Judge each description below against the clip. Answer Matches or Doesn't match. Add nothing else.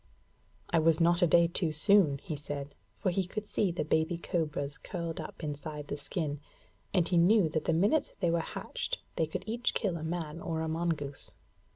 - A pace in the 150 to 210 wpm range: Matches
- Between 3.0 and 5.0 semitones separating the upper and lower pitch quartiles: Doesn't match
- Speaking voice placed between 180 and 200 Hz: Doesn't match